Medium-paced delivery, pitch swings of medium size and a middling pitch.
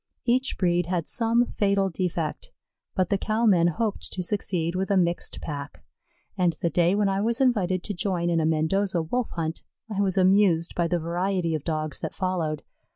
Yes: average, 190 wpm; average, 3.0 semitones; medium, 180 Hz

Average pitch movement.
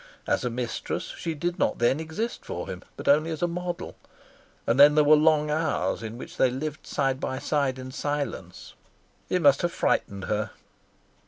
Yes: average, 3.6 semitones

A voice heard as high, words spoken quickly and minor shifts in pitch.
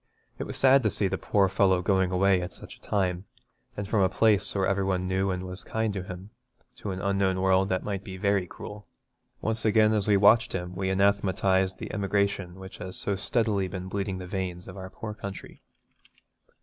No: very low, 95 Hz; fast, 210 wpm; narrow, 1.5 semitones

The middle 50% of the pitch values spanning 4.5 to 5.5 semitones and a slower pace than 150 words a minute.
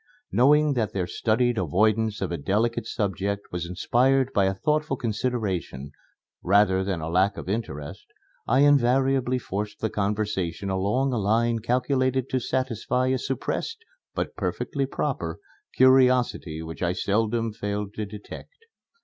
Yes: average, 4.8 semitones; average, 140 wpm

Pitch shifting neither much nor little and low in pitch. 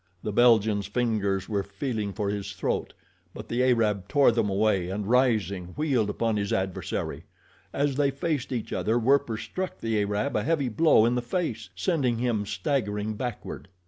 Yes: average, 3.7 semitones; low, 110 Hz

